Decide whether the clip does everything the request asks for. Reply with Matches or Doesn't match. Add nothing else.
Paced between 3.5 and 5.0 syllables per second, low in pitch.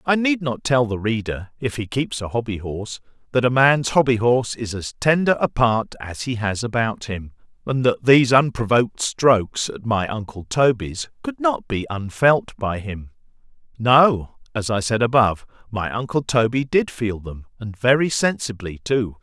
Matches